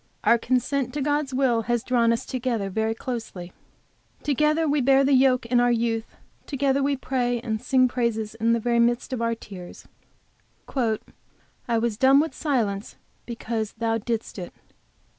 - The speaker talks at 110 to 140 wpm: No, average, 160 wpm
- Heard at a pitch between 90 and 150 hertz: No, high, 240 Hz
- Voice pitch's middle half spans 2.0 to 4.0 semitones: Yes, average, 2.8 semitones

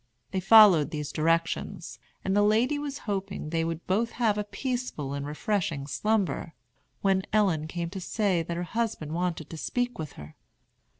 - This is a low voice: No, medium, 185 Hz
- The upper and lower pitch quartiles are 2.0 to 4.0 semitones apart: No, average, 5.1 semitones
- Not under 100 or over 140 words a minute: No, average, 165 wpm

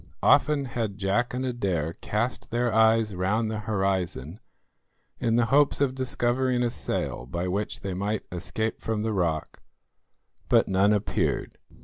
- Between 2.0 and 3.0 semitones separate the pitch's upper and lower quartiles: No, average, 4.0 semitones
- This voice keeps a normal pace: Yes, average, 145 wpm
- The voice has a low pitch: Yes, low, 110 Hz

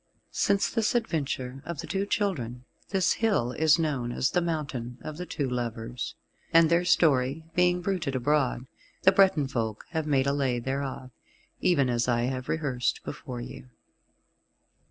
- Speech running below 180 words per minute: Yes, average, 155 wpm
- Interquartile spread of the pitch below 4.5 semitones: No, average, 5.2 semitones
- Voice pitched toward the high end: No, medium, 140 Hz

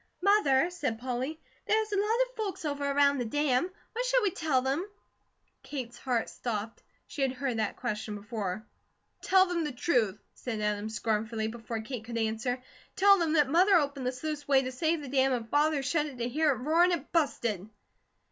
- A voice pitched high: Yes, very high, 270 Hz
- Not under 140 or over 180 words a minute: No, average, 195 wpm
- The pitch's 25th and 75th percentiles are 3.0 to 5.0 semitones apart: No, wide, 5.4 semitones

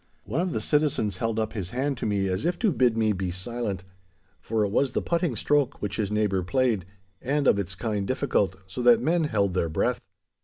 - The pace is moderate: No, fast, 220 wpm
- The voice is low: Yes, low, 110 Hz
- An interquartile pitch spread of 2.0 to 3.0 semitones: No, wide, 5.6 semitones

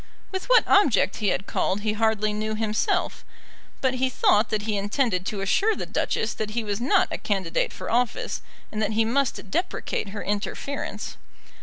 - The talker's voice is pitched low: No, high, 215 Hz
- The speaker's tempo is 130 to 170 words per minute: No, average, 180 wpm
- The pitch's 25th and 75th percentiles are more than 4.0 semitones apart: No, average, 3.2 semitones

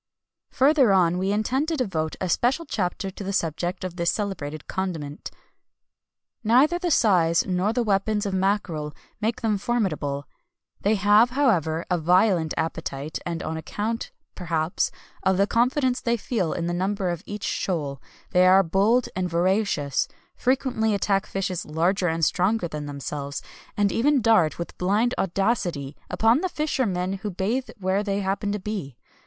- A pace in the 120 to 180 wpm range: Yes, average, 160 wpm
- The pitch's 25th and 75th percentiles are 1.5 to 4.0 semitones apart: No, average, 4.6 semitones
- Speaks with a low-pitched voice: No, high, 195 Hz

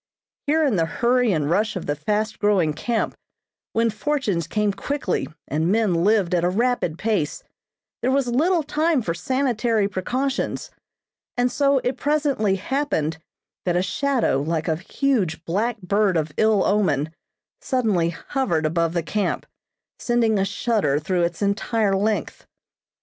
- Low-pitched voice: No, high, 210 Hz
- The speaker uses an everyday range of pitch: No, wide, 6.3 semitones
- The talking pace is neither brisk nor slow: Yes, average, 150 wpm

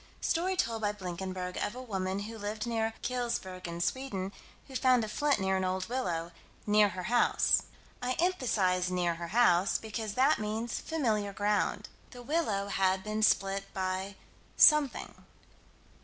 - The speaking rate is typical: Yes, average, 150 wpm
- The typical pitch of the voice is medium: No, high, 210 Hz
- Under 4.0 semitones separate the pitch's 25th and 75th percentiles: No, average, 4.5 semitones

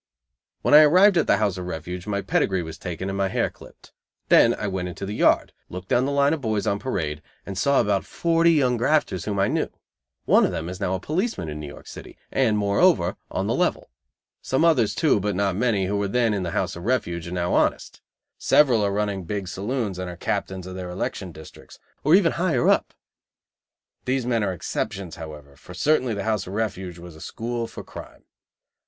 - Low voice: Yes, low, 100 Hz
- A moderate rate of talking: No, fast, 215 wpm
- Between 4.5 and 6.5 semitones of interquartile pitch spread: Yes, wide, 5.5 semitones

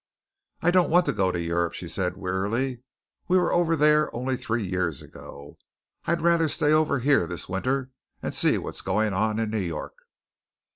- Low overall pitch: Yes, low, 115 Hz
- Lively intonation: Yes, wide, 8.6 semitones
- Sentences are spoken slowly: No, average, 185 wpm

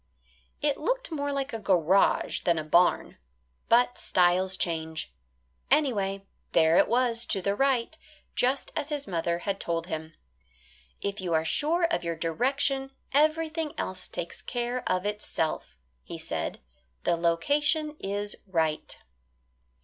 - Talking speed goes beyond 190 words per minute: No, slow, 135 wpm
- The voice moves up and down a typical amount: No, wide, 8.5 semitones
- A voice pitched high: Yes, high, 205 Hz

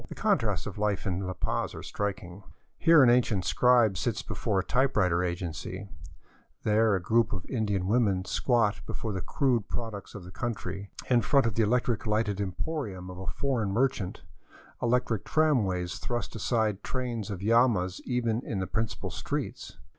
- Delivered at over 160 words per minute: Yes, average, 170 wpm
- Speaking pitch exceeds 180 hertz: No, low, 105 Hz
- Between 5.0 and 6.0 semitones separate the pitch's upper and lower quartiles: No, average, 4.1 semitones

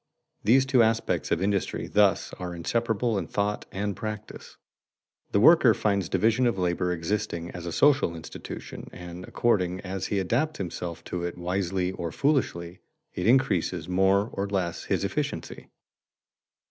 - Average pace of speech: Yes, average, 145 wpm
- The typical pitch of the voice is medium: No, very low, 95 Hz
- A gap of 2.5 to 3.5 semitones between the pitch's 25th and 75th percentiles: No, average, 4.0 semitones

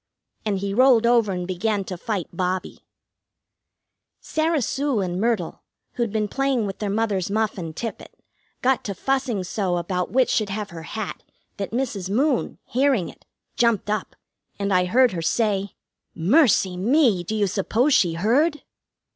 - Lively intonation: No, average, 4.5 semitones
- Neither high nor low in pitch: No, high, 210 Hz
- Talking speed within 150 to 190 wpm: Yes, average, 160 wpm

